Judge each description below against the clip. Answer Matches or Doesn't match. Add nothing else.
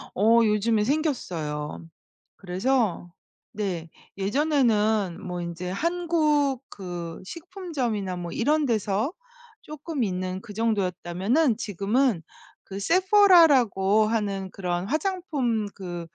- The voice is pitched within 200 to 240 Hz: Matches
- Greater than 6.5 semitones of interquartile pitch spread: Matches